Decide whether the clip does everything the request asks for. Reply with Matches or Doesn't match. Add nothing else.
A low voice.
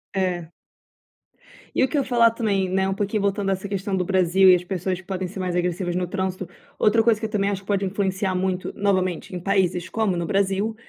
Doesn't match